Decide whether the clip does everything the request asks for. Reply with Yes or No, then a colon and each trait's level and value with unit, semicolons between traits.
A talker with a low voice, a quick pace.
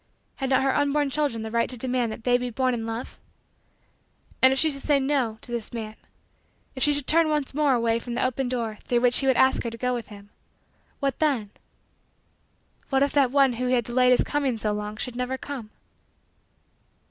No: very high, 250 Hz; fast, 215 wpm